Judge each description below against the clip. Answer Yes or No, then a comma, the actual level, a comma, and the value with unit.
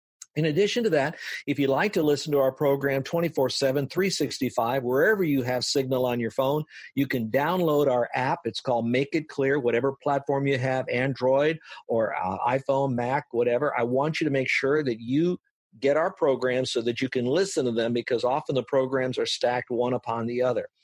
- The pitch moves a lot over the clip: No, narrow, 2.6 semitones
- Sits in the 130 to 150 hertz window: Yes, low, 135 Hz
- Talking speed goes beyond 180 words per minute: Yes, average, 200 wpm